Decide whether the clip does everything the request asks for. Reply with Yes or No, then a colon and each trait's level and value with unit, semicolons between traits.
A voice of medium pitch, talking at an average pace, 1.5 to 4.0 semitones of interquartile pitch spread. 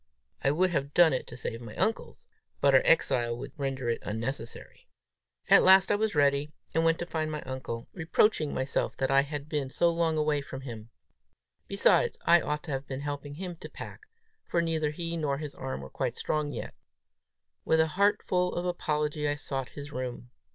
Yes: medium, 150 Hz; average, 195 wpm; average, 3.5 semitones